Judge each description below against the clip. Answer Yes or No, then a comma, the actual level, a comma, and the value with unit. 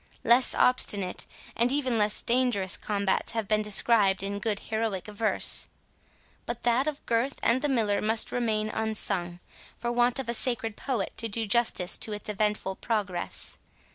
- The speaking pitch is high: Yes, high, 220 Hz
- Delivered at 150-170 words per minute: Yes, average, 160 wpm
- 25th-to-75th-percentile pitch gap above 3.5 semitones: No, average, 2.7 semitones